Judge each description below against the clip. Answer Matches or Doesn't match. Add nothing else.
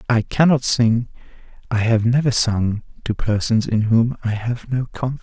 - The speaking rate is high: Doesn't match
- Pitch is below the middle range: Matches